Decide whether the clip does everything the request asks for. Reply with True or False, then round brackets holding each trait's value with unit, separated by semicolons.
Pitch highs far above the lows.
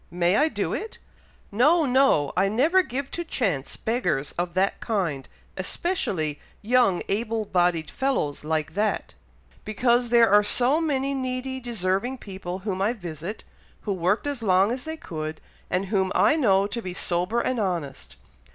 True (6.0 semitones)